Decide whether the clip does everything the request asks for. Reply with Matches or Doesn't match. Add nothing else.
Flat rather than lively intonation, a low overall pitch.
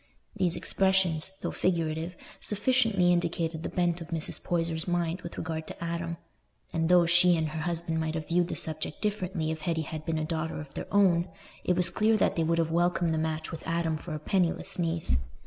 Doesn't match